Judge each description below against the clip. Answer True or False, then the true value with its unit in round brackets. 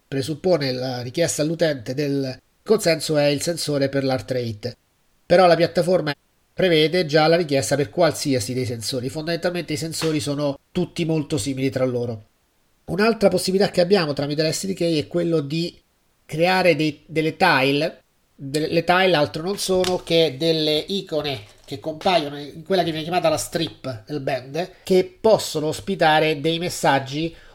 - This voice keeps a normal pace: True (150 wpm)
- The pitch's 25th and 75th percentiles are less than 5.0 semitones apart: True (3.8 semitones)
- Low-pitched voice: False (155 Hz)